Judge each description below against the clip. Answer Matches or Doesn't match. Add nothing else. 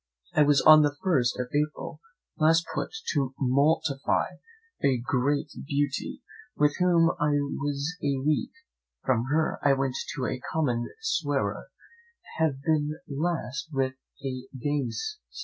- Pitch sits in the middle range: Matches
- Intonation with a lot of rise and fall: Doesn't match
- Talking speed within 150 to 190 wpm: Doesn't match